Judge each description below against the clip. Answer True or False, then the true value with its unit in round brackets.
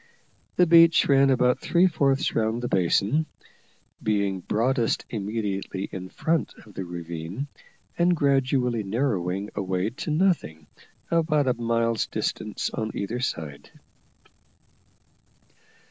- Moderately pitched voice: False (115 Hz)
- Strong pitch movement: True (6.2 semitones)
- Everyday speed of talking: False (115 wpm)